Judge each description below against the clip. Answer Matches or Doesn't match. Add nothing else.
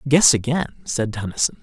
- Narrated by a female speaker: Doesn't match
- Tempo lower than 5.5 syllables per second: Matches